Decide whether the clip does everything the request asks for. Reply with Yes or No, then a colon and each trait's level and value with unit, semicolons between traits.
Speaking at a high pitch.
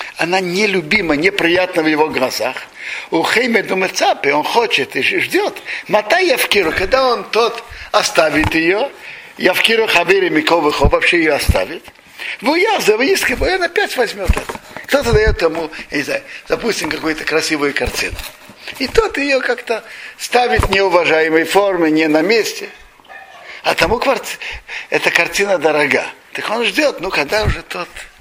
Yes: high, 200 Hz